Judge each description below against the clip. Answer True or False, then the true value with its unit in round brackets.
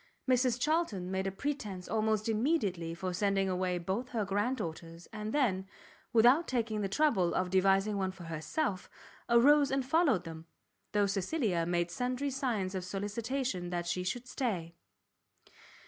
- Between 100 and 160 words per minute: True (150 wpm)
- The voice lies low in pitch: False (205 Hz)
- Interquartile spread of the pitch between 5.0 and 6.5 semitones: True (5.5 semitones)